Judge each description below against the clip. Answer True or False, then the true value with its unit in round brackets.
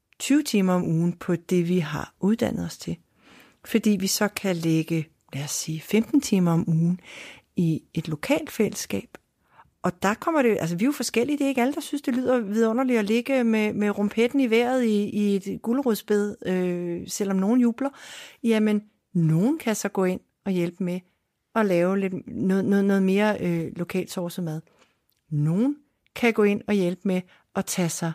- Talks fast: False (190 wpm)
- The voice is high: True (200 Hz)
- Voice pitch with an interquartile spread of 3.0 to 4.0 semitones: False (4.7 semitones)